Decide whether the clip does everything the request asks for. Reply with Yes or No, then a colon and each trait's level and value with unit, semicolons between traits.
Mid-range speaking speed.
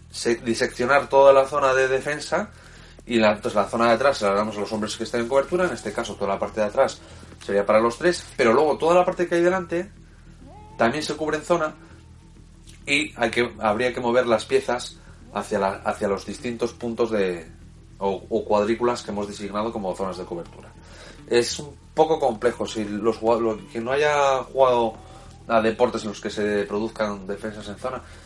No: fast, 200 wpm